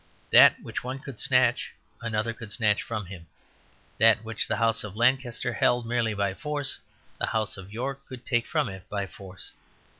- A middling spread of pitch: Yes, average, 3.3 semitones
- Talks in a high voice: No, low, 115 Hz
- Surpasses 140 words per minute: Yes, average, 180 wpm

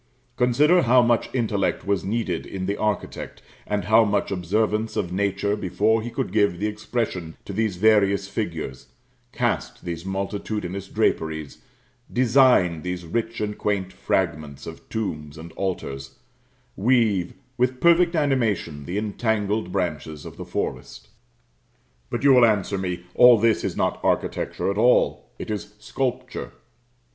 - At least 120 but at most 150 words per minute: Yes, average, 140 wpm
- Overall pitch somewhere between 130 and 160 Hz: No, low, 100 Hz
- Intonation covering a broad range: No, average, 4.1 semitones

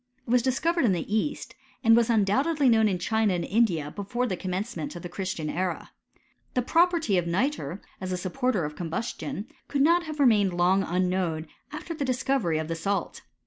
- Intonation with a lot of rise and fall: Yes, wide, 6.3 semitones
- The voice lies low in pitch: No, high, 205 Hz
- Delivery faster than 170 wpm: Yes, average, 190 wpm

